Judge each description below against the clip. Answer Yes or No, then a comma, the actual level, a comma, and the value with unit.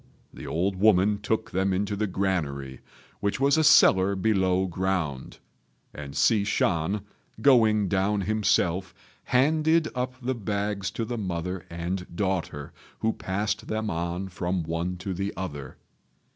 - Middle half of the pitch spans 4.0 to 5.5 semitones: No, average, 3.1 semitones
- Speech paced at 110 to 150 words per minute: Yes, average, 140 wpm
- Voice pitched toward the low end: Yes, very low, 95 Hz